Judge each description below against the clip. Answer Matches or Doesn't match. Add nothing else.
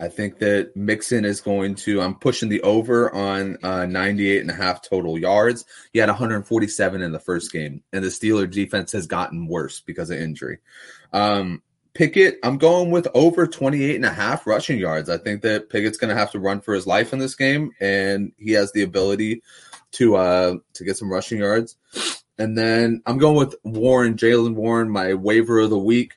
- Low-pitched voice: Matches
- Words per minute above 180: Matches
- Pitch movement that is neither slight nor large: Matches